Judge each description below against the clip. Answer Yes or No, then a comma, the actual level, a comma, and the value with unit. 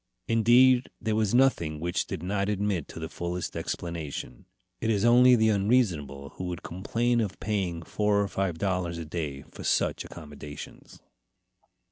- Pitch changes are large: No, average, 4.9 semitones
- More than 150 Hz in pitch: No, very low, 95 Hz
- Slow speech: No, average, 155 wpm